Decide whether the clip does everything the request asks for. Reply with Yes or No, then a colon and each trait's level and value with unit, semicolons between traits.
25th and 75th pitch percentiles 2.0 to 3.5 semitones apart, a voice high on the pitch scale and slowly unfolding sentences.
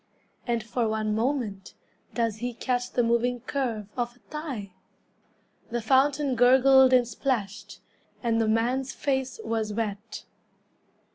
Yes: average, 2.9 semitones; high, 240 Hz; slow, 130 wpm